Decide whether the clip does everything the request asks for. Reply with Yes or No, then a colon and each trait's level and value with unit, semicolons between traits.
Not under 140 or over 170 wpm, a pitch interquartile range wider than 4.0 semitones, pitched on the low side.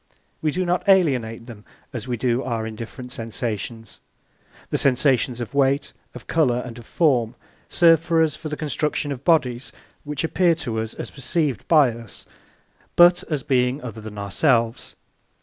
Yes: average, 165 wpm; average, 4.9 semitones; low, 130 Hz